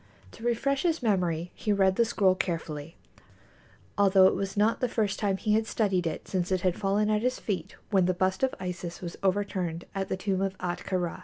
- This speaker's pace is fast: Yes, fast, 215 wpm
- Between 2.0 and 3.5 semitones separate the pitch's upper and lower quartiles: Yes, average, 2.8 semitones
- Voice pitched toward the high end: Yes, high, 195 Hz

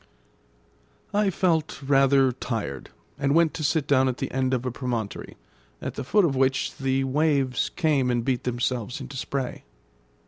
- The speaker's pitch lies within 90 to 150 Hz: Yes, low, 135 Hz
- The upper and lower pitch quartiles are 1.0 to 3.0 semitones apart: Yes, narrow, 2.4 semitones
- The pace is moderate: Yes, average, 165 wpm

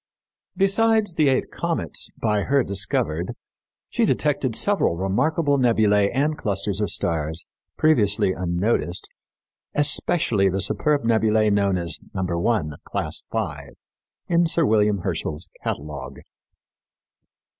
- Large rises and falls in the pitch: Yes, wide, 7.7 semitones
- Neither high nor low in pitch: No, low, 105 Hz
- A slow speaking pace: Yes, slow, 115 wpm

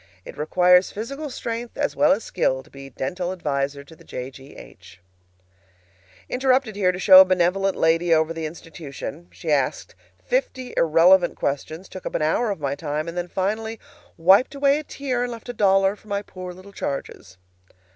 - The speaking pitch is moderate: Yes, medium, 180 Hz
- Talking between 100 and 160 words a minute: No, average, 180 wpm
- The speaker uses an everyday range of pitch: No, wide, 5.8 semitones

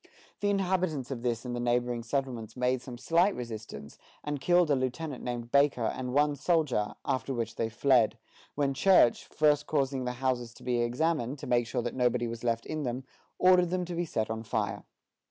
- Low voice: Yes, low, 125 Hz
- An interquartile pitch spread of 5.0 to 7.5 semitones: No, average, 3.8 semitones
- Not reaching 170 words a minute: No, average, 195 wpm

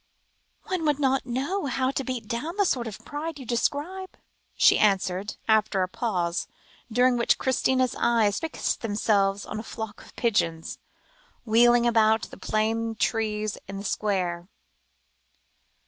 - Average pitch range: Yes, average, 3.9 semitones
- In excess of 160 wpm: No, average, 145 wpm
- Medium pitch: No, high, 230 Hz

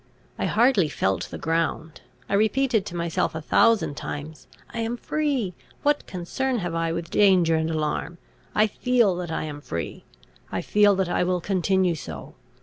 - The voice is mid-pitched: Yes, medium, 180 Hz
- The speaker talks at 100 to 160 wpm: No, average, 170 wpm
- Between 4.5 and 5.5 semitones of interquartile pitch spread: Yes, average, 5.2 semitones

